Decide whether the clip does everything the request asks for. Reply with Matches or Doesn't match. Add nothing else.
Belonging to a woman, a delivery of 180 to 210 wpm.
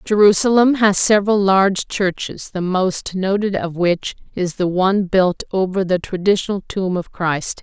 Doesn't match